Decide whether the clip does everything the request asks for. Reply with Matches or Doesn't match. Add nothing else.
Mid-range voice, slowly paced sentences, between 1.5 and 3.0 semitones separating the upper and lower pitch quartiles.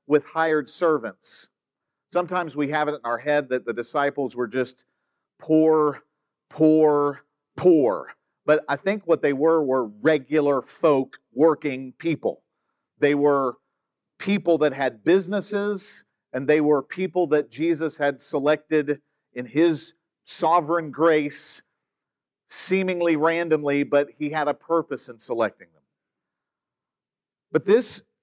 Matches